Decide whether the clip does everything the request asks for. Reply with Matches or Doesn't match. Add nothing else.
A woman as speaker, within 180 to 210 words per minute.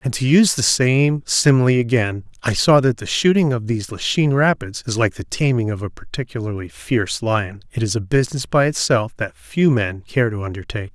Doesn't match